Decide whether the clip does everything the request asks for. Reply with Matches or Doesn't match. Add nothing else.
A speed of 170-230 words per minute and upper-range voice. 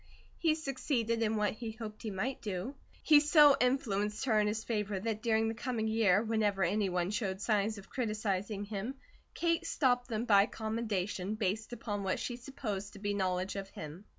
Matches